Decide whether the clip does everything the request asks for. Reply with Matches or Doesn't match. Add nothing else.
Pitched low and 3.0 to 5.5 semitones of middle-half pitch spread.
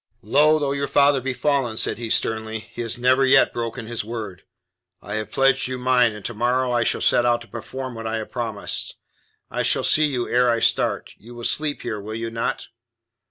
Doesn't match